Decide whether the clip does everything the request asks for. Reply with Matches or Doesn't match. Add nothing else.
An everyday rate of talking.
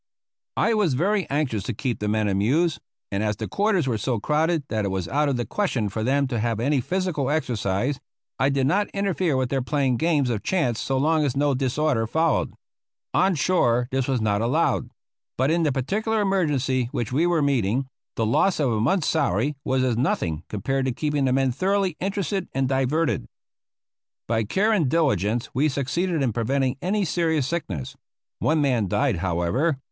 Matches